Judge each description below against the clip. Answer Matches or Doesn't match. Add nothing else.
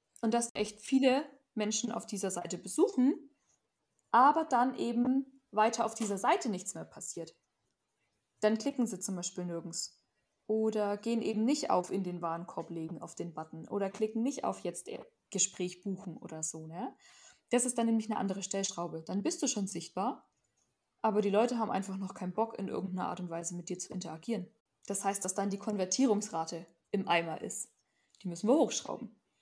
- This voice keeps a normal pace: Matches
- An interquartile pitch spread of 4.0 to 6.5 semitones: Matches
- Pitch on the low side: Doesn't match